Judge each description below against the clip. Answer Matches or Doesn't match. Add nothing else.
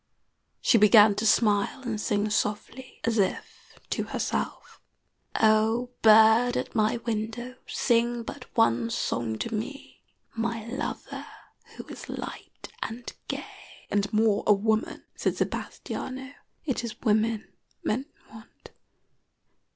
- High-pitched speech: Matches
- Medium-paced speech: Doesn't match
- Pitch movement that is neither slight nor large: Doesn't match